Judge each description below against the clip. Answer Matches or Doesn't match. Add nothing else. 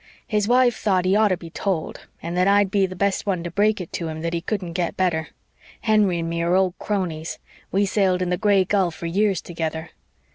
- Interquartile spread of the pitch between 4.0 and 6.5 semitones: Doesn't match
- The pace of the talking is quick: Matches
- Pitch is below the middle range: Doesn't match